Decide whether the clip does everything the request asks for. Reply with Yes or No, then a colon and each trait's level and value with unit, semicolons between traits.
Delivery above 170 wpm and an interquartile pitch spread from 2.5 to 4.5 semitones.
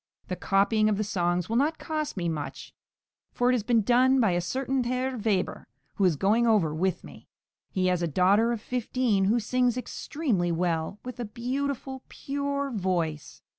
No: average, 180 wpm; wide, 5.6 semitones